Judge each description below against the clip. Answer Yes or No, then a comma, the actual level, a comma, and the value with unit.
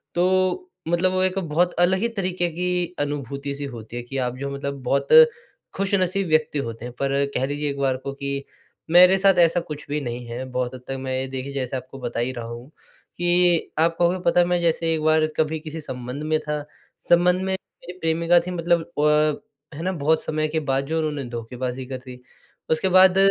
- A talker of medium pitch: Yes, medium, 155 Hz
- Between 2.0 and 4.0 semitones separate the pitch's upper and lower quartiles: No, average, 4.8 semitones